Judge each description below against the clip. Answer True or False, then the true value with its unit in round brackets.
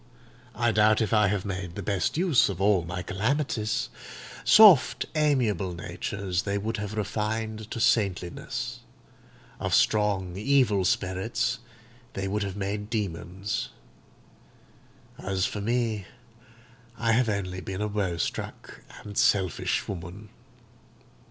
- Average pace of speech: False (125 wpm)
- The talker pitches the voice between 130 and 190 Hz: False (105 Hz)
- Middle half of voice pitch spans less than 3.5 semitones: True (2.8 semitones)